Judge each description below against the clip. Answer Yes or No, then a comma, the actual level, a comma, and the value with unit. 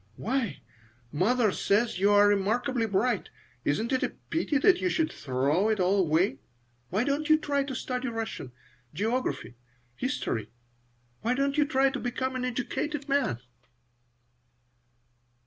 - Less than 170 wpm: Yes, average, 140 wpm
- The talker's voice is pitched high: Yes, high, 240 Hz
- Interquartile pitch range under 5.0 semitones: No, wide, 5.5 semitones